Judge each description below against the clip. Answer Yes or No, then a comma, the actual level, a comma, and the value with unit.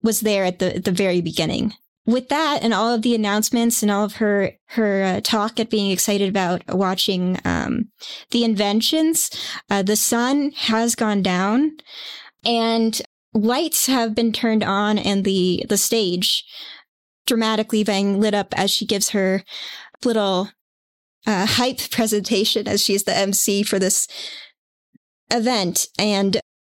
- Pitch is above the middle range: Yes, high, 215 Hz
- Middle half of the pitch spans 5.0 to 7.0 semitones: No, average, 2.8 semitones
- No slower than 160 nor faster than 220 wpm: No, average, 150 wpm